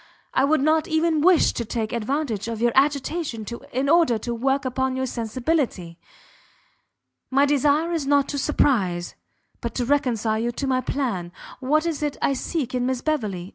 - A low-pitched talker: No, very high, 265 Hz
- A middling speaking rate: Yes, average, 175 wpm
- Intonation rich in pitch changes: No, average, 4.0 semitones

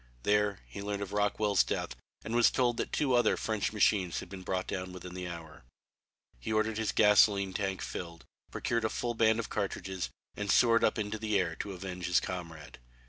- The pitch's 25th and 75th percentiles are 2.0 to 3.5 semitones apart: Yes, average, 3.0 semitones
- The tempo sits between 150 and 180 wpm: No, average, 195 wpm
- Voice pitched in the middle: No, low, 100 Hz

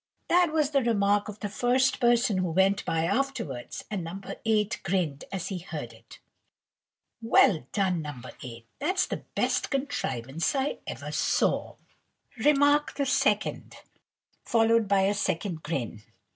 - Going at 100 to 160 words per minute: Yes, average, 145 wpm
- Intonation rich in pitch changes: Yes, wide, 7.6 semitones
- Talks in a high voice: Yes, high, 200 Hz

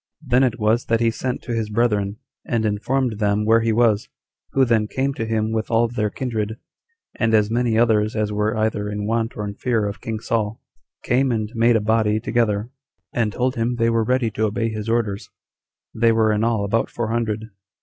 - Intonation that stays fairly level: Yes, narrow, 1.8 semitones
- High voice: No, low, 110 Hz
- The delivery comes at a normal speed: No, fast, 210 wpm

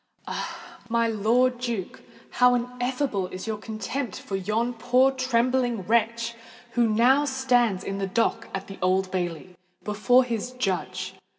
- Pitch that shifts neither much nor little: Yes, average, 4.1 semitones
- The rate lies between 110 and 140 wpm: Yes, slow, 135 wpm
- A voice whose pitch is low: No, high, 230 Hz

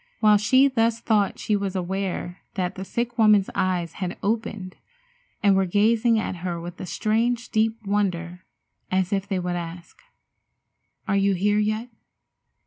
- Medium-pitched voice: No, high, 200 Hz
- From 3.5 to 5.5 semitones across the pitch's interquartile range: No, average, 3.1 semitones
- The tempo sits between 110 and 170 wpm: Yes, average, 155 wpm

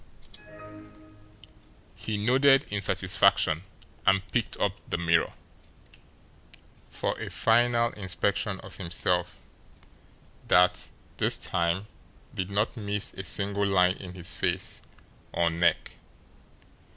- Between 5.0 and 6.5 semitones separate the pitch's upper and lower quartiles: No, average, 2.7 semitones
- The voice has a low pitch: Yes, very low, 95 Hz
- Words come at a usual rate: No, slow, 105 wpm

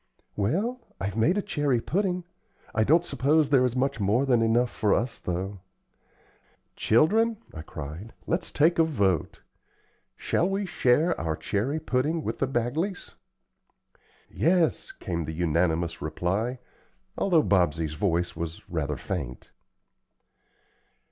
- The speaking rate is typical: No, slow, 130 wpm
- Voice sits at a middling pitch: No, low, 120 Hz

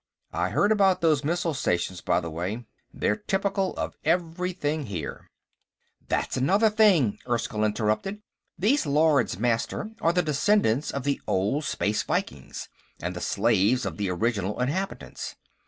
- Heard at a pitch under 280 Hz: Yes, medium, 140 Hz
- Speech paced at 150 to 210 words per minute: No, average, 140 wpm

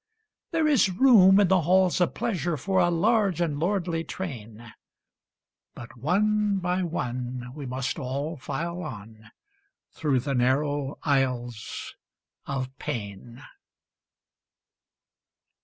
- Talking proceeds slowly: Yes, slow, 110 wpm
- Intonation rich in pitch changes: Yes, wide, 6.5 semitones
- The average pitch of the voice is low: No, medium, 150 Hz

